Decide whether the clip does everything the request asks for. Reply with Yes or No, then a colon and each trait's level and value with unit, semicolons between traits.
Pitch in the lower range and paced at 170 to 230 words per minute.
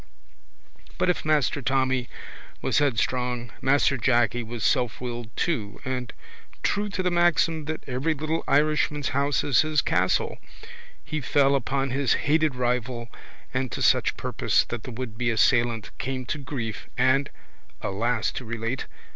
No: low, 130 Hz; average, 140 wpm